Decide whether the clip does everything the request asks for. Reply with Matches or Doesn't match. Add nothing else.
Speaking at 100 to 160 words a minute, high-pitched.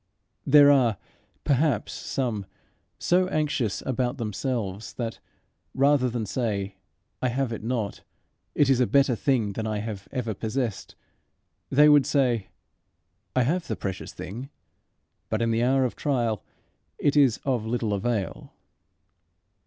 Doesn't match